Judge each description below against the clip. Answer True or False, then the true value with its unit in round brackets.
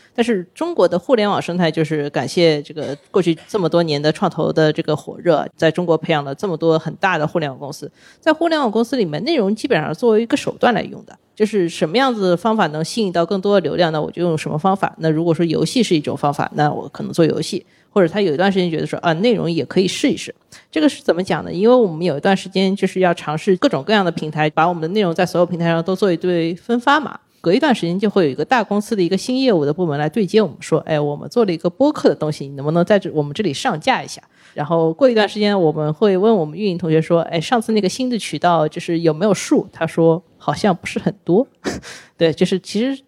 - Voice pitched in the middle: True (175 Hz)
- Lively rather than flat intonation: False (4.7 semitones)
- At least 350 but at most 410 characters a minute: True (390 characters per minute)